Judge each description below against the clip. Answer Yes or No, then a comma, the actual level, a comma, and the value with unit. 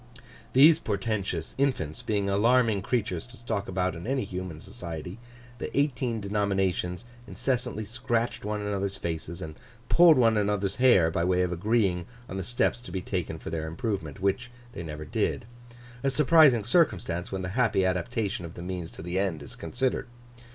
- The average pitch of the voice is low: Yes, low, 100 Hz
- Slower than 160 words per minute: No, average, 165 wpm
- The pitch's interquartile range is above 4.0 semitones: Yes, average, 5.0 semitones